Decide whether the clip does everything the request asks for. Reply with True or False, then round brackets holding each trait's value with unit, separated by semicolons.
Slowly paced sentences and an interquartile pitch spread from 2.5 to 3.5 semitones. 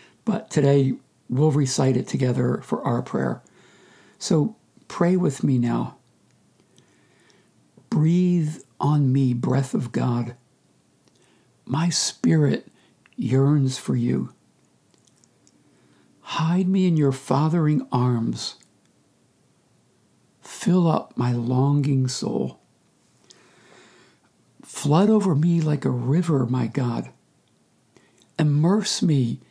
False (95 wpm; 4.5 semitones)